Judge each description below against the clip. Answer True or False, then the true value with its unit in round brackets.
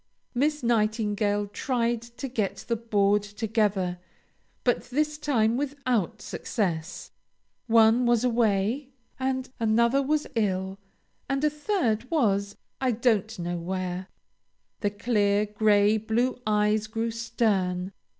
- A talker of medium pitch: False (220 Hz)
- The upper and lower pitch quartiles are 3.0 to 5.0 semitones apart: True (3.3 semitones)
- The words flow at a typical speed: False (115 wpm)